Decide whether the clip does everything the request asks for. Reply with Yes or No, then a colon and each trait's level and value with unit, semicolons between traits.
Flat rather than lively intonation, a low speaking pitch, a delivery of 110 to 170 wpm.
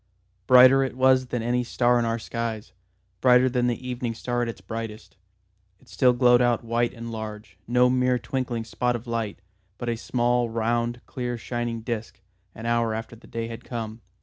No: narrow, 1.3 semitones; low, 120 Hz; average, 185 wpm